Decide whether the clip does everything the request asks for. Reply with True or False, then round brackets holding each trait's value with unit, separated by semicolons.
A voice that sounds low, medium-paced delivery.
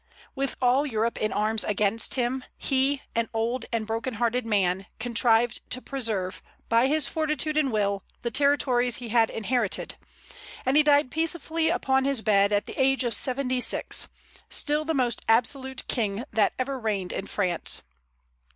False (245 Hz; 160 wpm)